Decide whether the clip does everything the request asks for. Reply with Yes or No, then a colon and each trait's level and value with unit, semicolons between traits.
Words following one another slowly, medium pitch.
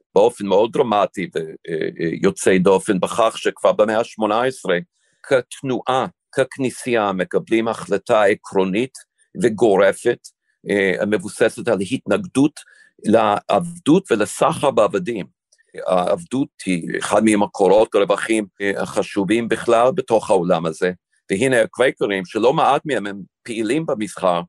No: slow, 95 wpm; low, 115 Hz